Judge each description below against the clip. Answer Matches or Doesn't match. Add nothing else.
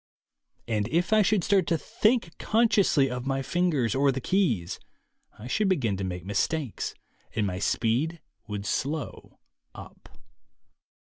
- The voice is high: Doesn't match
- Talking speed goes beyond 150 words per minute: Doesn't match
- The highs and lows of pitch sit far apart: Matches